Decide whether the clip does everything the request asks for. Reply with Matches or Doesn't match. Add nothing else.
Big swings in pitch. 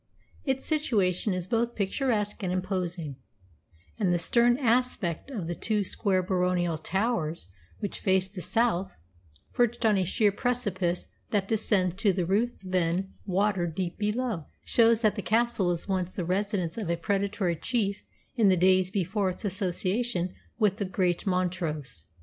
Doesn't match